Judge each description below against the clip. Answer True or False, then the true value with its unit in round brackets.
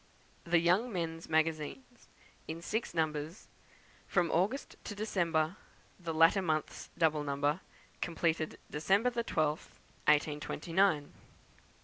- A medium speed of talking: False (105 wpm)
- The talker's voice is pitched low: False (165 Hz)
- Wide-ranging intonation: False (3.5 semitones)